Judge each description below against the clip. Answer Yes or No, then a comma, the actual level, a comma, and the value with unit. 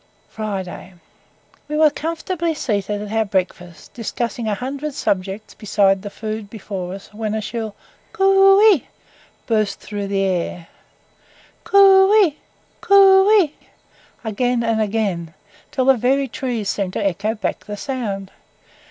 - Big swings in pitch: Yes, wide, 6.5 semitones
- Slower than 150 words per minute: Yes, slow, 135 wpm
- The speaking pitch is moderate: No, high, 220 Hz